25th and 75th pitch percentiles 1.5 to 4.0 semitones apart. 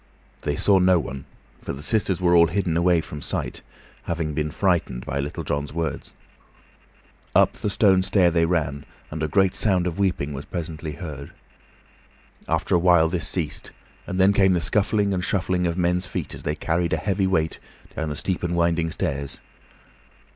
Yes: average, 3.0 semitones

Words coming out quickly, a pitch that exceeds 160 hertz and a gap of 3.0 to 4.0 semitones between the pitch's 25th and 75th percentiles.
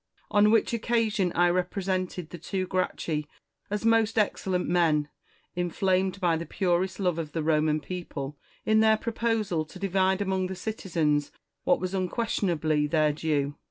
No: average, 160 wpm; medium, 185 Hz; average, 3.7 semitones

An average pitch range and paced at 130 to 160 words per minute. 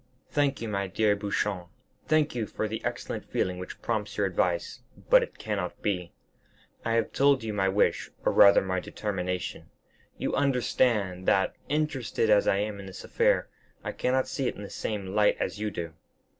No: average, 3.2 semitones; average, 185 wpm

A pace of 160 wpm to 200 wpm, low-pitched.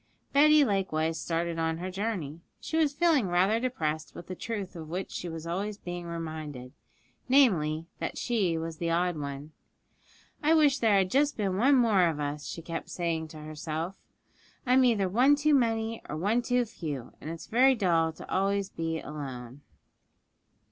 No: average, 175 wpm; medium, 180 Hz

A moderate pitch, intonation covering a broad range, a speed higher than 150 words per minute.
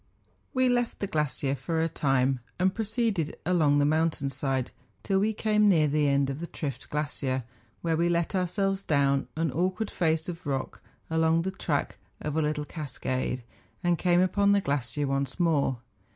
No: medium, 160 Hz; average, 4.6 semitones; average, 180 wpm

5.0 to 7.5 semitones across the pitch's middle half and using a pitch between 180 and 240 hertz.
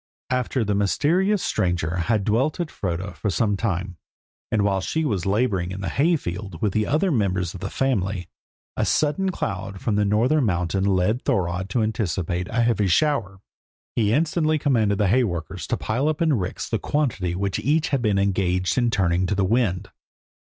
No: wide, 5.4 semitones; low, 105 Hz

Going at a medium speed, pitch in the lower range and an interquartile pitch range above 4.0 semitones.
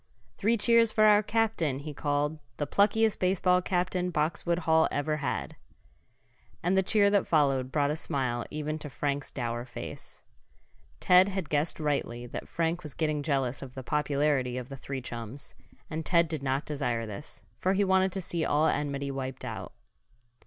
No: average, 175 wpm; medium, 150 Hz; average, 4.8 semitones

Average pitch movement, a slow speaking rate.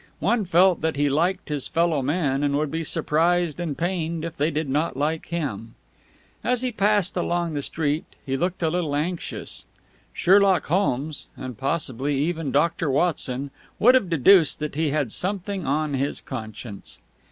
No: average, 3.7 semitones; average, 165 wpm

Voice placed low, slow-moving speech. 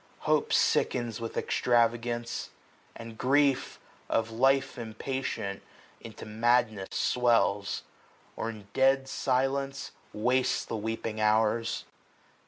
Yes: low, 120 Hz; slow, 95 wpm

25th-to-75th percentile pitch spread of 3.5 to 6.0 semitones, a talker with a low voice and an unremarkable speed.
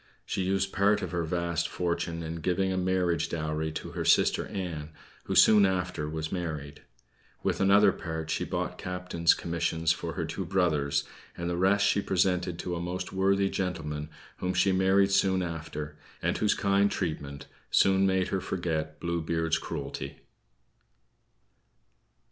No: average, 2.9 semitones; very low, 90 Hz; average, 155 wpm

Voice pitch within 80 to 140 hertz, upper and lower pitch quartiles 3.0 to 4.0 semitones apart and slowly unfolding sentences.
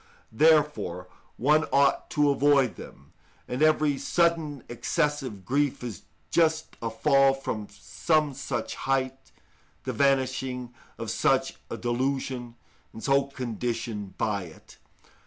Yes: low, 135 Hz; average, 3.7 semitones; slow, 120 wpm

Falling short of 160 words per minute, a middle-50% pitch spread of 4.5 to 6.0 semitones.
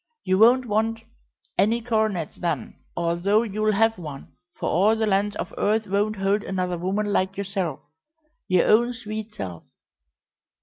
No: average, 145 wpm; average, 3.0 semitones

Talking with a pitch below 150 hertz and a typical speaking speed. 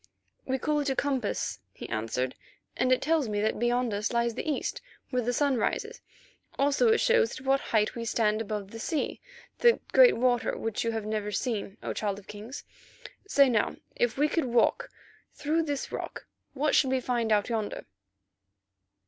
No: high, 245 Hz; average, 185 wpm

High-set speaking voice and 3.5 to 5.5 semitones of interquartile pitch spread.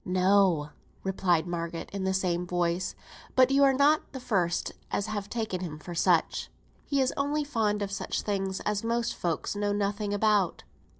Yes: high, 200 Hz; average, 4.0 semitones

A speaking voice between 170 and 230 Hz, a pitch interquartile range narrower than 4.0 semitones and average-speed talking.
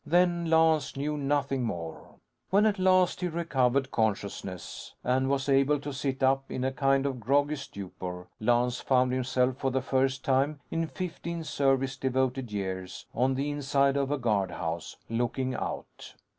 No: low, 135 Hz; narrow, 2.6 semitones; average, 155 wpm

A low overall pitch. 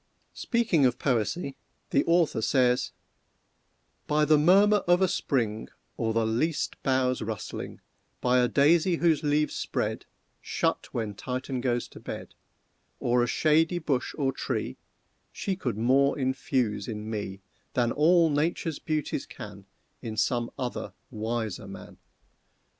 Yes: low, 130 Hz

